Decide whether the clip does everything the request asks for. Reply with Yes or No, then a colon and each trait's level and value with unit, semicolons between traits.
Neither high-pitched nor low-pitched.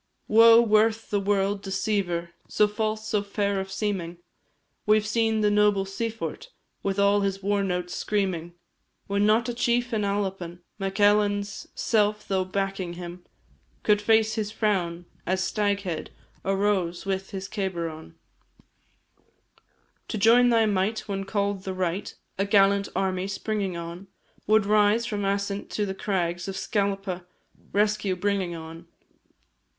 No: high, 200 Hz